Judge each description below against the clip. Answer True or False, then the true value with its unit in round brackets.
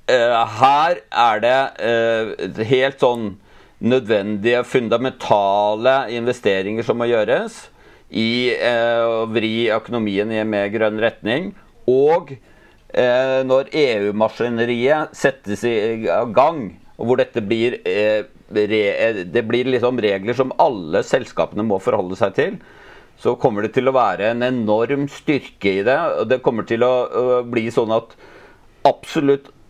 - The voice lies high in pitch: False (115 Hz)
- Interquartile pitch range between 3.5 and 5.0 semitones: False (2.7 semitones)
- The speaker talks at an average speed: False (125 wpm)